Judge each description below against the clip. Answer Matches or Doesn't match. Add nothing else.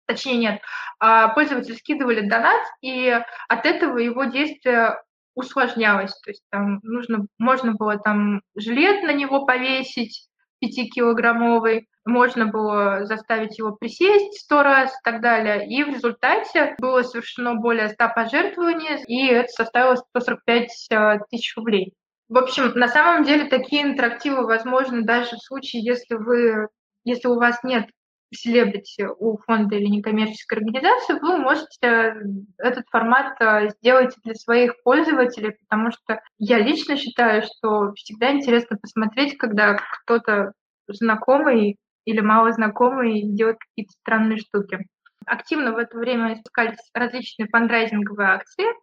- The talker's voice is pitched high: Matches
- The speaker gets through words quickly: Doesn't match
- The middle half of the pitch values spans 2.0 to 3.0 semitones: Matches